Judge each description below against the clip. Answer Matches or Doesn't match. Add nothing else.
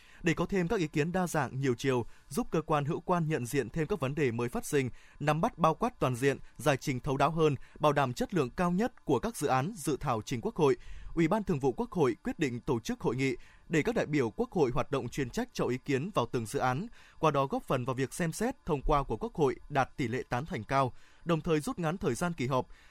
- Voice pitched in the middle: Matches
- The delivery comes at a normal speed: Doesn't match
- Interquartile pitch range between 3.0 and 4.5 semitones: Doesn't match